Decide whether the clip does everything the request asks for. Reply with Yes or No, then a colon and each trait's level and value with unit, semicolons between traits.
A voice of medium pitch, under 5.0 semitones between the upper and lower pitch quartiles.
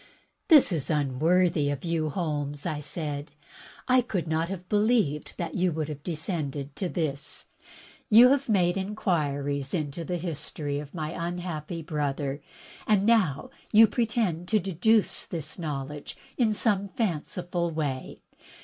Yes: medium, 165 Hz; average, 4.4 semitones